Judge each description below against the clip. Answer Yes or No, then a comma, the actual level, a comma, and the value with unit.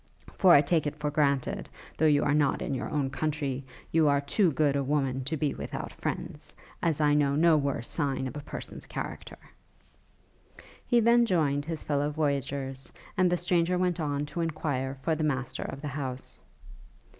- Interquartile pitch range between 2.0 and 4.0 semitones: Yes, narrow, 2.4 semitones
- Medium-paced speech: Yes, average, 185 wpm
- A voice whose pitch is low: No, medium, 145 Hz